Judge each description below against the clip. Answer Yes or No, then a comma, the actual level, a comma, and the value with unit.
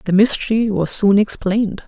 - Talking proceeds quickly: No, average, 160 wpm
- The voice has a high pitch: Yes, high, 205 Hz